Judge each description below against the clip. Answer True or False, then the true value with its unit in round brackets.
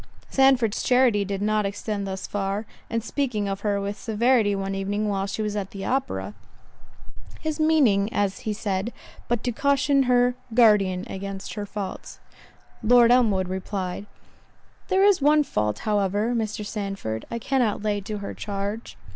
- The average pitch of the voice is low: False (210 Hz)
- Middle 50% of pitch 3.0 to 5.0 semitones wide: True (3.5 semitones)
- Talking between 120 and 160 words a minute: True (155 wpm)